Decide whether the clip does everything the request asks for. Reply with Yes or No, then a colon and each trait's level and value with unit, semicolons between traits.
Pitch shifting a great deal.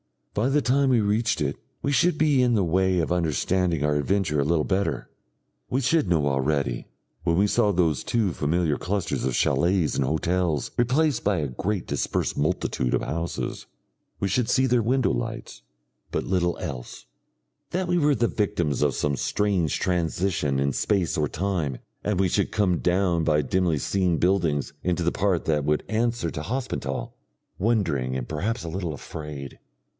Yes: wide, 5.7 semitones